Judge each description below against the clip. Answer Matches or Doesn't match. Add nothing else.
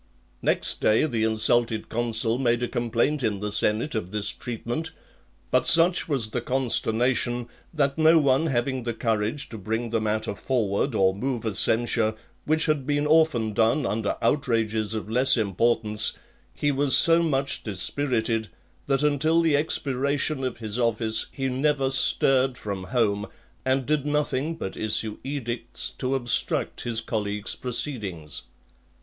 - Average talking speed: Matches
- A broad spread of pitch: Doesn't match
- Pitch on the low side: Matches